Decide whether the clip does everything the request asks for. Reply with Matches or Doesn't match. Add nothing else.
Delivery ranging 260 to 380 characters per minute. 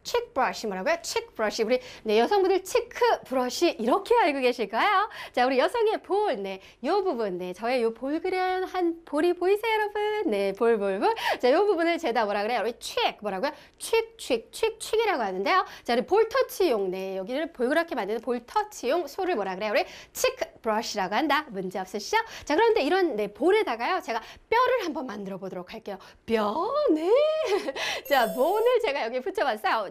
Matches